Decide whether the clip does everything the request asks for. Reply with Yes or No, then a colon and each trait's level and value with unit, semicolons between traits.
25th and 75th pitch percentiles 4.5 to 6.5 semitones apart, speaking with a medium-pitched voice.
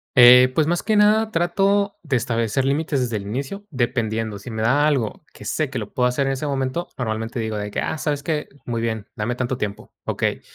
No: average, 5.1 semitones; low, 130 Hz